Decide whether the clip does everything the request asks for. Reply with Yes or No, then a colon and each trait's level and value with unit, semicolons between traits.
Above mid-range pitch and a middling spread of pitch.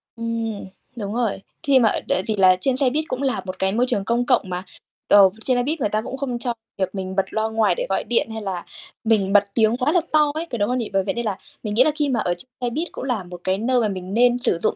Yes: high, 230 Hz; average, 4.4 semitones